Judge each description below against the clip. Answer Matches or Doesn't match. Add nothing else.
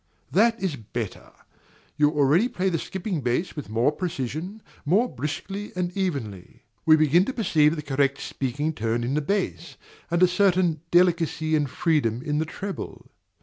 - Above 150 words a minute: Matches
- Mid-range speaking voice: Matches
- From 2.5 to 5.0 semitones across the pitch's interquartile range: Matches